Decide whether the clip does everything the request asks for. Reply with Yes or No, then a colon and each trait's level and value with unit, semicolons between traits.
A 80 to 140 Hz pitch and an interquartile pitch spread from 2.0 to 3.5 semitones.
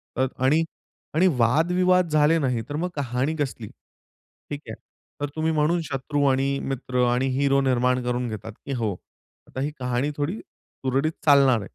Yes: low, 135 Hz; average, 3.2 semitones